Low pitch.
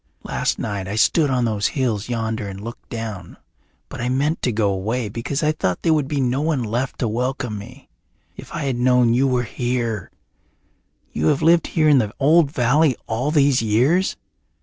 Yes: low, 125 Hz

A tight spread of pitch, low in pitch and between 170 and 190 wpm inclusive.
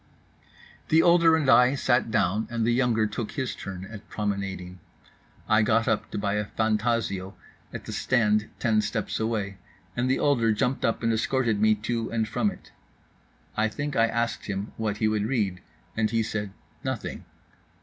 Yes: narrow, 2.3 semitones; low, 110 Hz; average, 175 wpm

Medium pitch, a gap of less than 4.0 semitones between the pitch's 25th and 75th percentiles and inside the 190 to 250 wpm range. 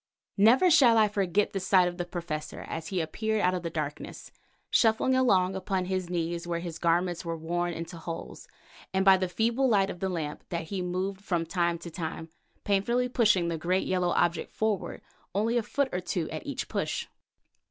Yes: medium, 180 Hz; average, 3.2 semitones; average, 195 wpm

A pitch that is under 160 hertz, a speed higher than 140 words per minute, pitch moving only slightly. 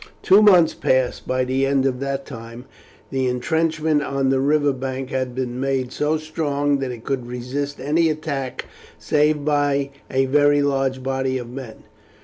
Yes: low, 135 Hz; average, 165 wpm; narrow, 2.0 semitones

